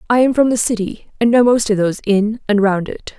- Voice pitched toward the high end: Yes, high, 220 Hz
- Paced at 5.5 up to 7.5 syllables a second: Yes, 5.6 syllables/s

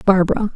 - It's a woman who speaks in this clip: Yes, female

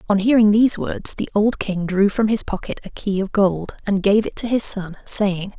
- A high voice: Yes, high, 205 Hz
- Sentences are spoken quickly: Yes, fast, 235 wpm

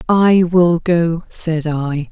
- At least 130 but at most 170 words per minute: Yes, average, 140 wpm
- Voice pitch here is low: No, medium, 170 Hz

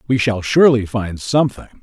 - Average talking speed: Yes, average, 165 wpm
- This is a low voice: Yes, low, 115 Hz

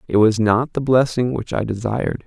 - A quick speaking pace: Yes, fast, 210 wpm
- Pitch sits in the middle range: No, low, 115 Hz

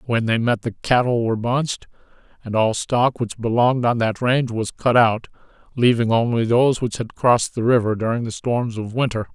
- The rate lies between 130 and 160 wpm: No, average, 200 wpm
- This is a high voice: No, low, 115 Hz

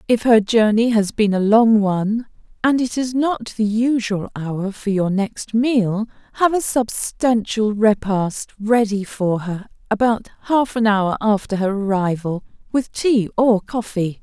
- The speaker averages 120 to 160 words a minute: Yes, average, 155 wpm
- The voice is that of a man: No, female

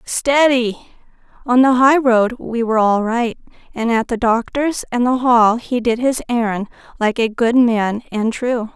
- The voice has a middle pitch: No, high, 235 Hz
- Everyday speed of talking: Yes, average, 170 wpm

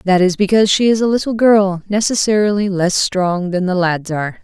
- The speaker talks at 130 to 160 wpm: No, fast, 205 wpm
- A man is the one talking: No, female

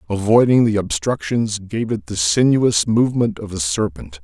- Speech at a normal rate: Yes, average, 155 wpm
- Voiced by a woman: No, male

